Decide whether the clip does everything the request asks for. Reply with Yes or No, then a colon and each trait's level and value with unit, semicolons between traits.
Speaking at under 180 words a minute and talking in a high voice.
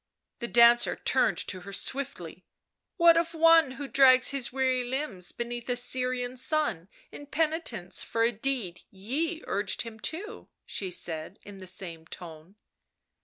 Yes: average, 155 wpm; high, 245 Hz